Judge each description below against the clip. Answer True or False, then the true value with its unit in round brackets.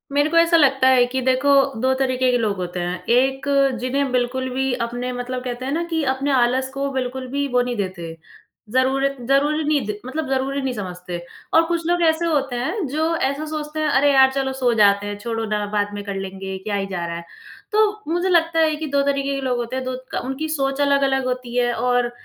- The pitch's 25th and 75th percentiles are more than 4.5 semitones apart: False (2.8 semitones)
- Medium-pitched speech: False (260 Hz)